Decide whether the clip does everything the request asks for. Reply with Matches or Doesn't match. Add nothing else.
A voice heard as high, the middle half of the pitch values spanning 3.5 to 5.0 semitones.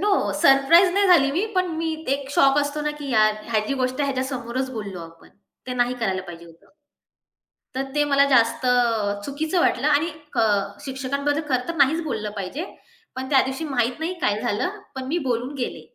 Matches